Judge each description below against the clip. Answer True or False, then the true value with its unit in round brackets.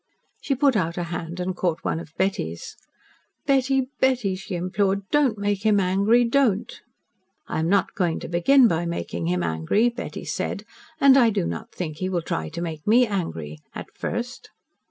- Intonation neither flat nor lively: False (6.0 semitones)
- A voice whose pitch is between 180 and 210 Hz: True (190 Hz)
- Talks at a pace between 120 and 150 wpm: False (180 wpm)